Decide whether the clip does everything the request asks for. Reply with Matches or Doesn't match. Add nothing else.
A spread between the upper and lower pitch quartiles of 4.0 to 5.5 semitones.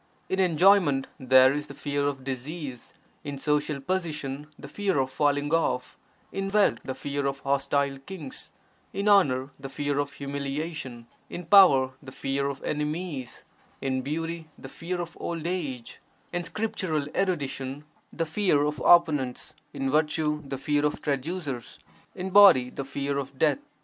Doesn't match